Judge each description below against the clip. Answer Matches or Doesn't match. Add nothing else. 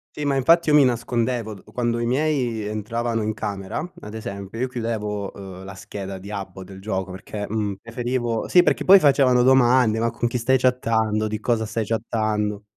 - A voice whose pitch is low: Matches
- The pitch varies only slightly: Doesn't match